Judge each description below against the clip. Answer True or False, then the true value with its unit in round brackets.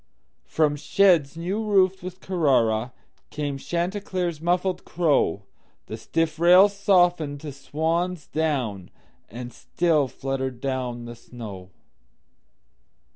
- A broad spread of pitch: True (6.0 semitones)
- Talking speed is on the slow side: True (90 wpm)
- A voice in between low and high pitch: True (155 Hz)